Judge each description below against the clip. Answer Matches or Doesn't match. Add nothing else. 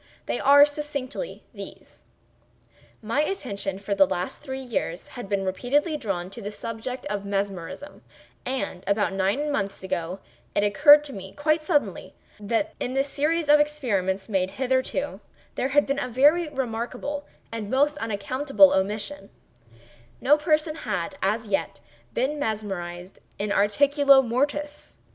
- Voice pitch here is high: Matches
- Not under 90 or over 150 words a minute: Matches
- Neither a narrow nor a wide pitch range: Doesn't match